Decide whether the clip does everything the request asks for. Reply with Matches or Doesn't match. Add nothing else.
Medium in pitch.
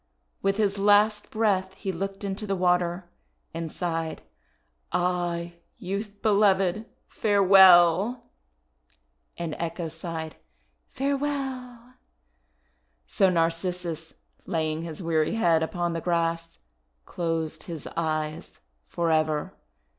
Matches